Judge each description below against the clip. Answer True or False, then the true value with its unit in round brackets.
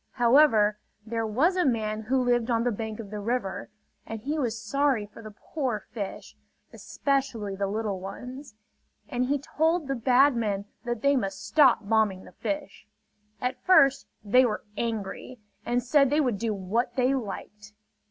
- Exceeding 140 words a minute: True (170 wpm)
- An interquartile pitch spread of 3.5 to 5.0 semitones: True (4.1 semitones)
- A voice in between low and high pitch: False (235 Hz)